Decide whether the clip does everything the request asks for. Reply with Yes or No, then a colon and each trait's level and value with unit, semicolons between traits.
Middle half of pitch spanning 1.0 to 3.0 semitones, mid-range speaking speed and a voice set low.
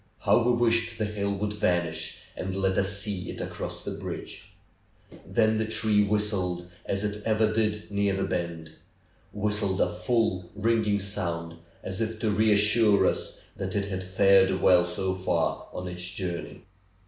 Yes: narrow, 2.5 semitones; average, 160 wpm; low, 100 Hz